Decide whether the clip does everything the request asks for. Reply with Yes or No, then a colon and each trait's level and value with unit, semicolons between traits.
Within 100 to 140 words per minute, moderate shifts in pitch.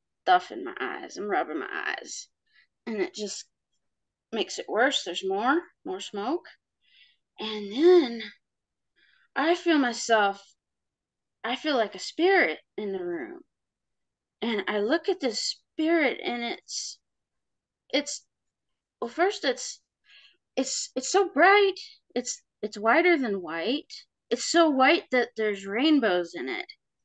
No: slow, 135 wpm; wide, 8.0 semitones